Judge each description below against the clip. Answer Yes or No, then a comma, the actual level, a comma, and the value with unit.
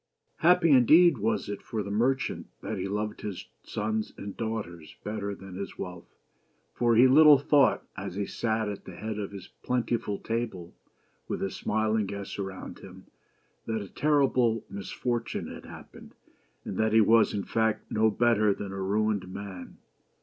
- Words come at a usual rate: Yes, average, 170 wpm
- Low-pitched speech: Yes, low, 110 Hz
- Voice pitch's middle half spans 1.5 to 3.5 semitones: Yes, average, 2.8 semitones